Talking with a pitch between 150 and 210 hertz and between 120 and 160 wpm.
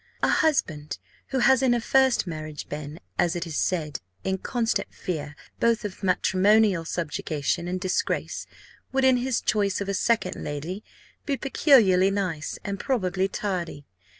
Yes: high, 190 Hz; average, 150 wpm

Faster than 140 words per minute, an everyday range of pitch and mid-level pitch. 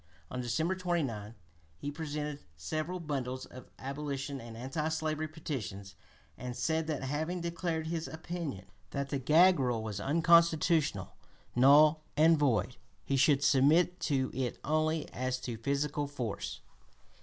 No: slow, 135 wpm; average, 3.7 semitones; medium, 145 Hz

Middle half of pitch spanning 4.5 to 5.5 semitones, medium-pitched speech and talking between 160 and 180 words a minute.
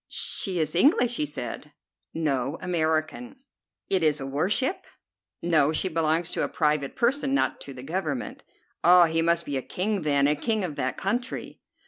Yes: average, 4.8 semitones; medium, 165 Hz; average, 175 wpm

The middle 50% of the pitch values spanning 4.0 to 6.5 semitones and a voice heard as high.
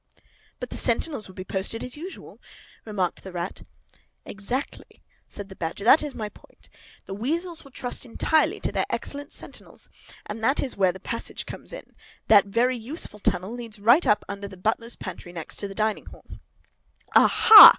Yes: average, 4.8 semitones; high, 220 Hz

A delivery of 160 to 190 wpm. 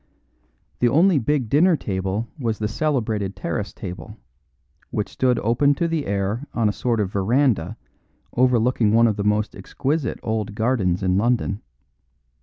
No: average, 150 wpm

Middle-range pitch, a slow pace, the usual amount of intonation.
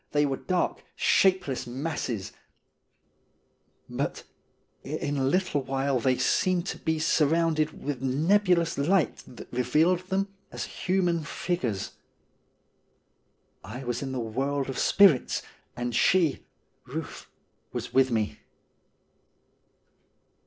Yes: medium, 145 Hz; slow, 110 wpm; average, 4.9 semitones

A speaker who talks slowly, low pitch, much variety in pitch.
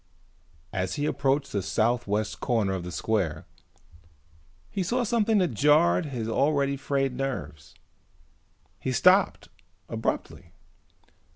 Yes: slow, 115 wpm; low, 125 Hz; wide, 6.8 semitones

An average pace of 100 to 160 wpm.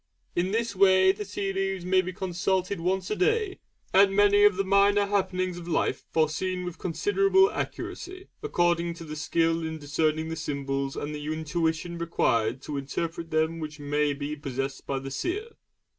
No: average, 175 wpm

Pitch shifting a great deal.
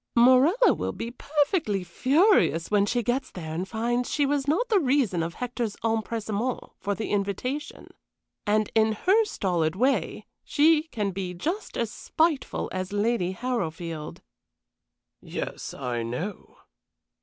Yes: wide, 6.6 semitones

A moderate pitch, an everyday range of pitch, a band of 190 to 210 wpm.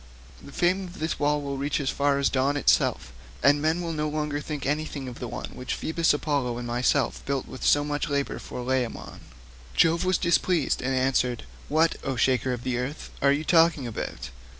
Yes: medium, 145 Hz; average, 3.1 semitones; average, 200 wpm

